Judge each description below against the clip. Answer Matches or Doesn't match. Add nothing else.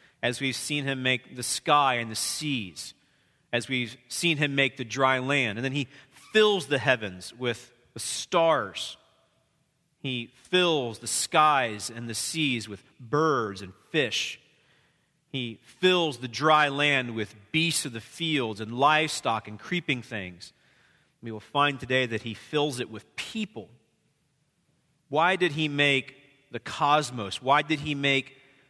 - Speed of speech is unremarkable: Matches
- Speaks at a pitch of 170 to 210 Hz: Doesn't match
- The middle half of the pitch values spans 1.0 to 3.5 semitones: Doesn't match